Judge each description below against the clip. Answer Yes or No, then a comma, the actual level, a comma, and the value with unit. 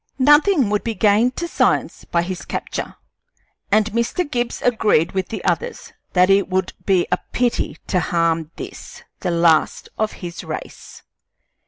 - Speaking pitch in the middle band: No, high, 205 Hz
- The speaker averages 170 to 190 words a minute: No, average, 155 wpm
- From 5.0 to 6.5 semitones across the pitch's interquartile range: Yes, average, 5.3 semitones